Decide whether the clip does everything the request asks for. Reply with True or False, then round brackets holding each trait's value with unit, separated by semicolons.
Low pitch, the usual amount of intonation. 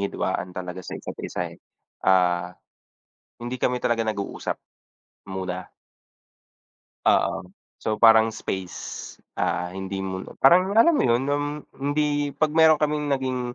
False (120 Hz; 7.4 semitones)